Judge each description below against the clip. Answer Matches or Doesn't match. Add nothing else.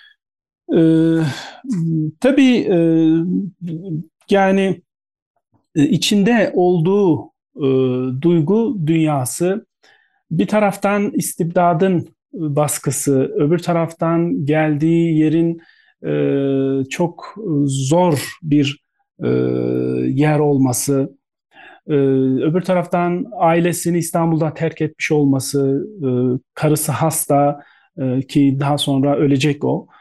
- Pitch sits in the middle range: Matches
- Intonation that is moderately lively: Matches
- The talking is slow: Matches